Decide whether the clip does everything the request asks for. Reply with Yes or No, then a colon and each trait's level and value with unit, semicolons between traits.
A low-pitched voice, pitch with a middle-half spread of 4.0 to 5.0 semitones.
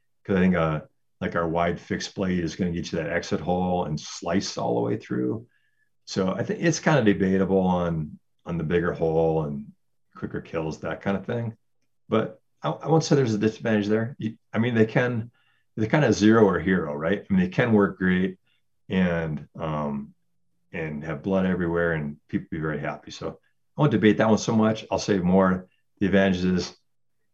Yes: very low, 95 Hz; average, 4.6 semitones